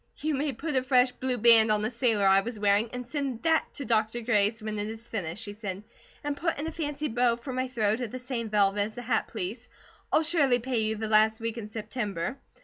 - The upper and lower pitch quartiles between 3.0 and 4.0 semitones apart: Yes, average, 3.3 semitones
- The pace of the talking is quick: Yes, fast, 240 wpm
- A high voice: Yes, high, 230 Hz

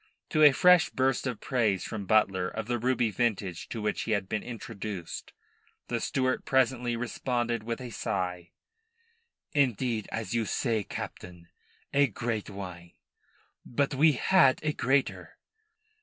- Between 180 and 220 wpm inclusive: No, average, 140 wpm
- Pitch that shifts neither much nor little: Yes, average, 4.3 semitones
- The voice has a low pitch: Yes, low, 115 Hz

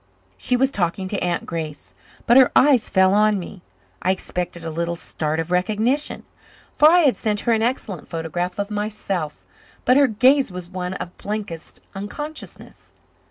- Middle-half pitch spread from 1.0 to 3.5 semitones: No, average, 5.2 semitones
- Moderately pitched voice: No, high, 200 Hz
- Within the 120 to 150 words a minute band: No, average, 165 wpm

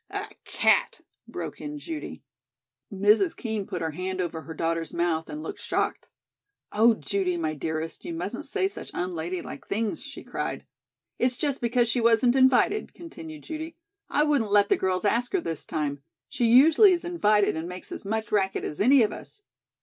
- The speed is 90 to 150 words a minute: No, average, 180 wpm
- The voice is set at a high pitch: Yes, high, 220 Hz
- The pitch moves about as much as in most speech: No, wide, 8.6 semitones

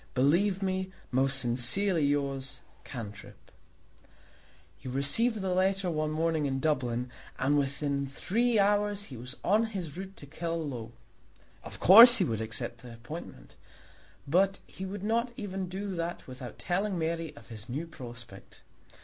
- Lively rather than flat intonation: Yes, wide, 6.5 semitones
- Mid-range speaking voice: Yes, medium, 160 Hz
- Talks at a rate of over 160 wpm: No, average, 145 wpm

